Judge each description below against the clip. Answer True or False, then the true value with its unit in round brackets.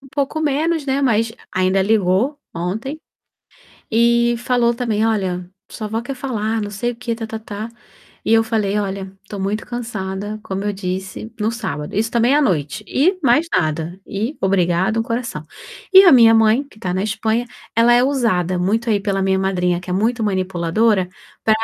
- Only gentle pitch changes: False (3.9 semitones)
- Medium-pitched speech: False (220 Hz)